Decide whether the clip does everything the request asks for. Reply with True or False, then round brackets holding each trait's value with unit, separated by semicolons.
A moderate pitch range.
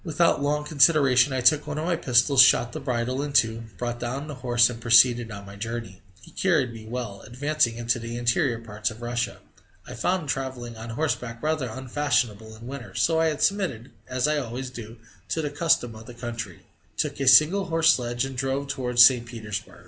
True (3.8 semitones)